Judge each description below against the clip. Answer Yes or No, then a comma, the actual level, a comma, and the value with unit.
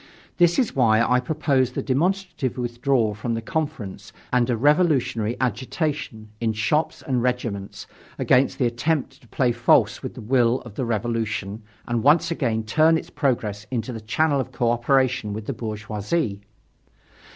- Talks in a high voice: No, low, 125 Hz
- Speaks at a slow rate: No, average, 155 wpm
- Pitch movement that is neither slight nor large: Yes, average, 3.9 semitones